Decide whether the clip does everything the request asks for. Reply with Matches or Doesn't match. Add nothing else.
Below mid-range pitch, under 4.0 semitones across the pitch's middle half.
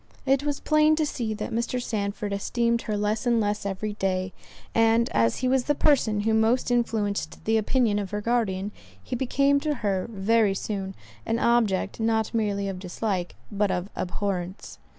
Doesn't match